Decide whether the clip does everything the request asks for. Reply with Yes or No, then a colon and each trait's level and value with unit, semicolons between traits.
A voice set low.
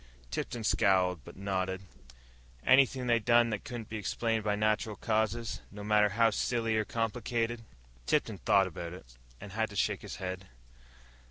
Yes: low, 110 Hz